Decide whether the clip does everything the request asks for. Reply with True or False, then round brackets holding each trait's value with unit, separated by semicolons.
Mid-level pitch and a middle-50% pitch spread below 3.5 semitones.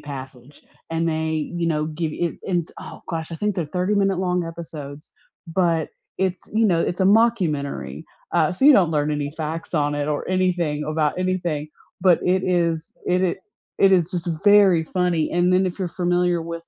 True (170 Hz; 2.8 semitones)